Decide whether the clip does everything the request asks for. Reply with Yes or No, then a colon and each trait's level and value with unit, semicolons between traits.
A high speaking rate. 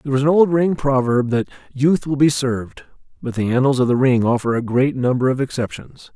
Yes: fast, 225 wpm